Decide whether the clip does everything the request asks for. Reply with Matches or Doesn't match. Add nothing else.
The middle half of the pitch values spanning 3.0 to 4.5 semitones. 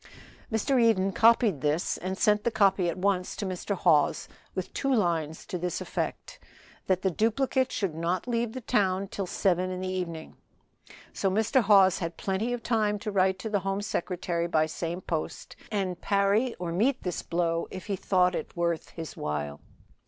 Matches